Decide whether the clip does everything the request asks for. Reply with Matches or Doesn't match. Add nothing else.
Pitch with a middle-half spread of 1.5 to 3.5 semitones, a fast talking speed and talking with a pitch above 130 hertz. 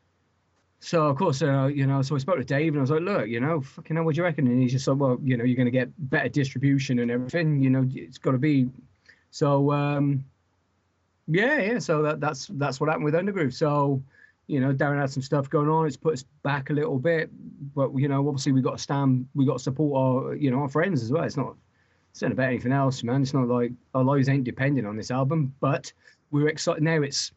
Matches